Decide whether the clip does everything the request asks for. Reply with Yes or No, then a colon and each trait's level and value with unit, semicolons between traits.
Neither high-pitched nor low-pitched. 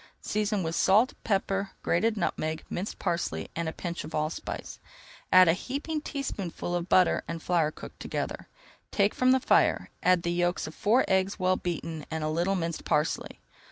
Yes: medium, 180 Hz